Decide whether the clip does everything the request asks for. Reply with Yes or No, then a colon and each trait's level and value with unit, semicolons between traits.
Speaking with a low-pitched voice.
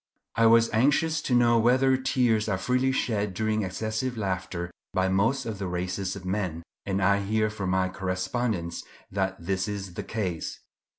Yes: low, 100 Hz